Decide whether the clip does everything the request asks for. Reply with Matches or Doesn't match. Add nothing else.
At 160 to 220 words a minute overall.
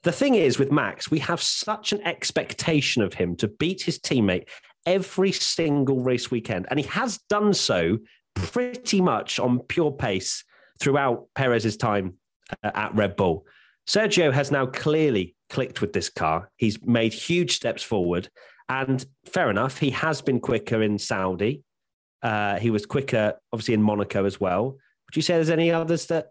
Matches